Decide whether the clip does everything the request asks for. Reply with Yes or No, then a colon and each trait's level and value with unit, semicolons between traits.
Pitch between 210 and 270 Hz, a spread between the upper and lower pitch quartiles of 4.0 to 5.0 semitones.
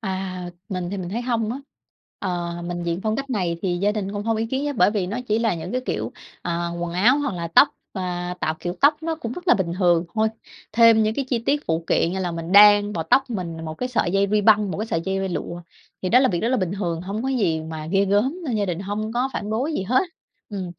No: high, 200 Hz; average, 4.5 semitones